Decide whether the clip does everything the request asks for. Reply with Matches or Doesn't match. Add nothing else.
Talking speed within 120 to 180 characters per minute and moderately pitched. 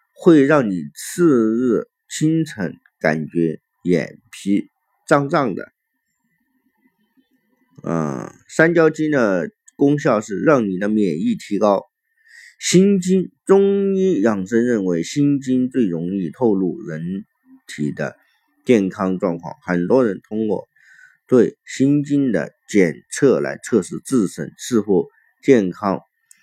Matches